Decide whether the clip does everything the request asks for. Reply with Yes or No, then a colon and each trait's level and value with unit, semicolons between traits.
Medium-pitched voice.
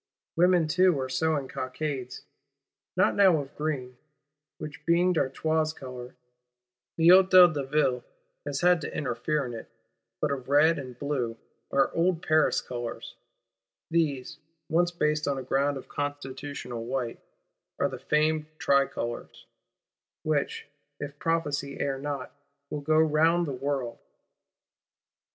Yes: medium, 145 Hz